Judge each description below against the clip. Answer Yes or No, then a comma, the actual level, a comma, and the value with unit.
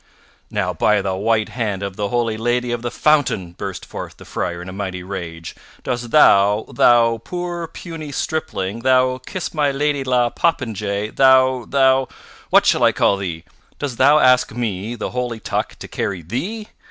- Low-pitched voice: Yes, low, 120 Hz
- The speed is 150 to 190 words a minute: Yes, average, 175 wpm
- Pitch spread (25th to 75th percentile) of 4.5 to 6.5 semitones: Yes, average, 4.8 semitones